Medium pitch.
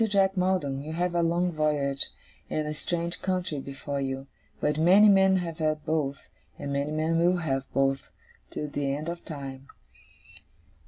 Yes: medium, 155 Hz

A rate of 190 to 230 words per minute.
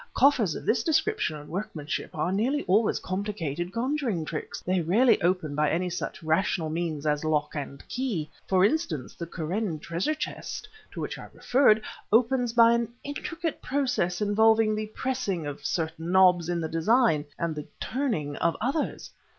No: average, 165 wpm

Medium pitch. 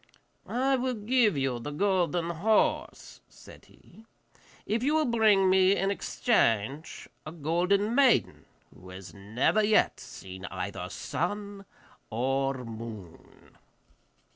Yes: medium, 175 Hz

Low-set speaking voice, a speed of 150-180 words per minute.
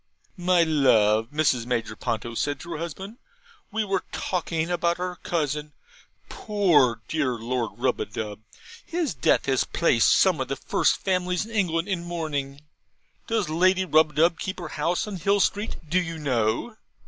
No: medium, 165 Hz; average, 155 wpm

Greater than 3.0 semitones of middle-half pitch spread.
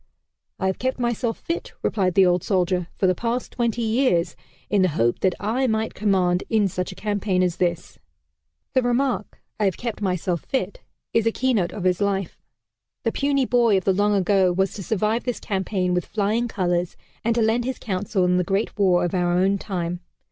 Yes: average, 3.9 semitones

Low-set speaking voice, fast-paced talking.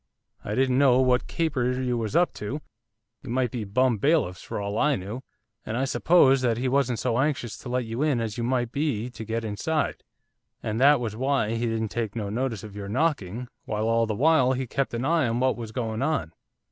Yes: low, 125 Hz; fast, 225 wpm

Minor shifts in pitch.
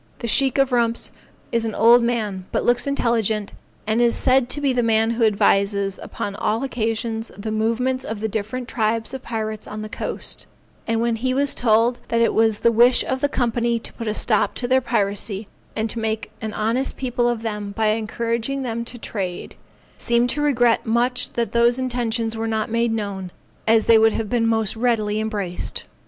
Yes: narrow, 1.8 semitones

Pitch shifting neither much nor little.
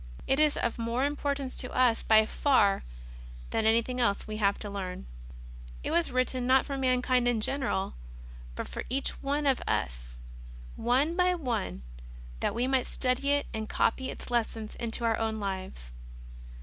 Yes: average, 3.6 semitones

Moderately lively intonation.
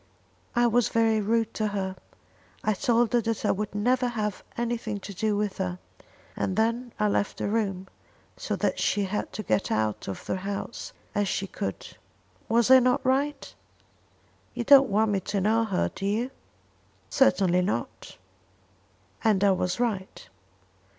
Yes: average, 3.3 semitones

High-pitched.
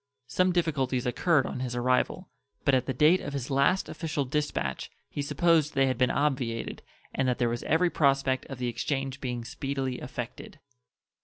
No: low, 135 Hz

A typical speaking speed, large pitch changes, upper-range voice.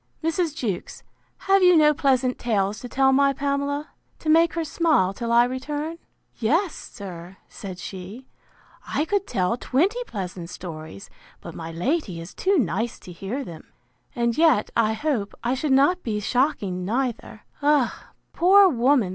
Yes: average, 155 wpm; wide, 7.3 semitones; very high, 255 Hz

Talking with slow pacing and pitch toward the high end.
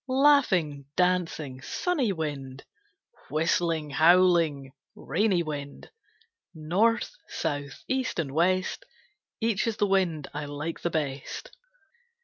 No: slow, 105 wpm; medium, 165 Hz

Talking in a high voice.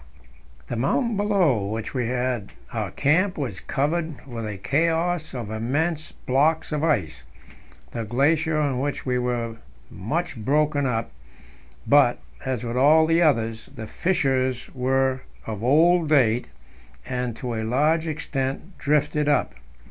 No: low, 135 Hz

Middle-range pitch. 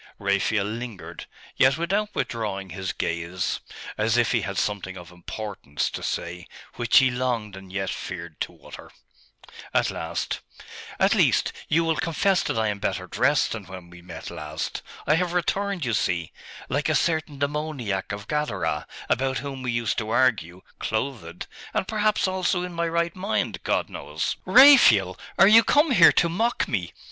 No: low, 120 Hz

